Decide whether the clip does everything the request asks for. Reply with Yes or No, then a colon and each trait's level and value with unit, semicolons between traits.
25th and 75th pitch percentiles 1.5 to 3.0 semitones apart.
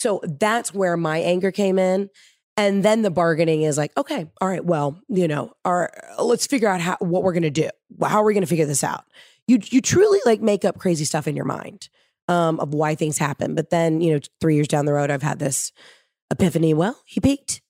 No: average, 4.3 semitones